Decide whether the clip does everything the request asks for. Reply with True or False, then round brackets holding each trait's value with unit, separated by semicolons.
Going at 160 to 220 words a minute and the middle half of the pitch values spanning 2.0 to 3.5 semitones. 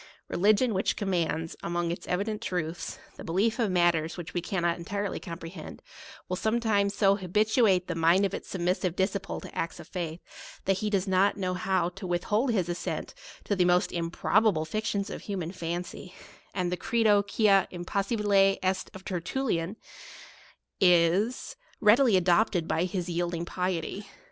True (165 wpm; 2.8 semitones)